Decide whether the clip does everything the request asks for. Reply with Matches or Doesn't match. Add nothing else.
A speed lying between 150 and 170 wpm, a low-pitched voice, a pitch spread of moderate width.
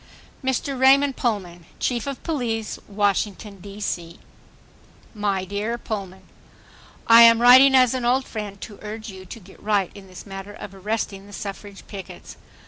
Doesn't match